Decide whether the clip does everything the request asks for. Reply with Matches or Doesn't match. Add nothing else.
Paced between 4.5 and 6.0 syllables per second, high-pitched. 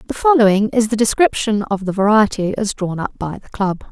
Matches